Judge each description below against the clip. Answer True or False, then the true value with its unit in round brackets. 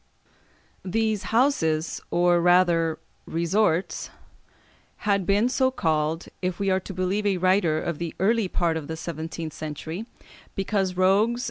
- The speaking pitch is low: False (180 Hz)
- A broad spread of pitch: False (3.6 semitones)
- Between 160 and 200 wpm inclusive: False (135 wpm)